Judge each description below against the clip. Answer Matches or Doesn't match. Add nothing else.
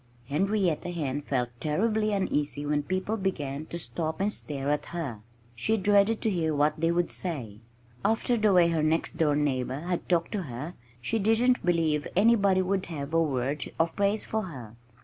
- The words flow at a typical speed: Matches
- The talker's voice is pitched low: Doesn't match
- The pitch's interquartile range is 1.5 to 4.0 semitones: Doesn't match